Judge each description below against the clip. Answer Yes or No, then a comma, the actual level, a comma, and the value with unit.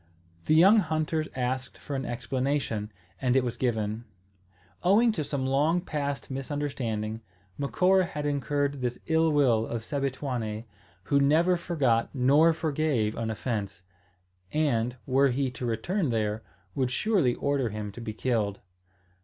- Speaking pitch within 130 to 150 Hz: Yes, low, 135 Hz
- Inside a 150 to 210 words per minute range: No, average, 140 wpm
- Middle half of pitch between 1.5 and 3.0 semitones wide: No, average, 4.6 semitones